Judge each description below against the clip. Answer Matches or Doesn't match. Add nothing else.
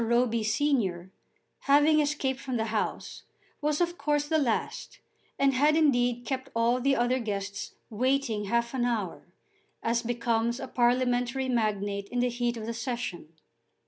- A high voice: Matches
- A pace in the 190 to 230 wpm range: Doesn't match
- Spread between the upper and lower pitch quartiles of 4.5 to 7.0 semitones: Doesn't match